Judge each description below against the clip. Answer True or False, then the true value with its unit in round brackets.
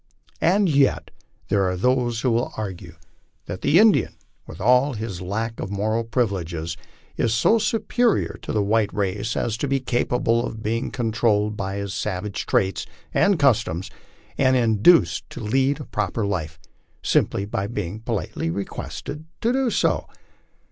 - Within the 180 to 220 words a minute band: False (150 wpm)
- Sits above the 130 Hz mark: False (110 Hz)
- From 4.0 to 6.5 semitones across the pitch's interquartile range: True (4.8 semitones)